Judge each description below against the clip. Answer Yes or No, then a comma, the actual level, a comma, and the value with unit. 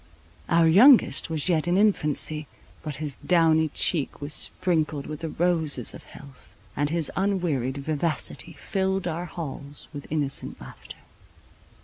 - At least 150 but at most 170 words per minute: No, slow, 135 wpm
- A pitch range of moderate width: Yes, average, 3.2 semitones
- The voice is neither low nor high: Yes, medium, 160 Hz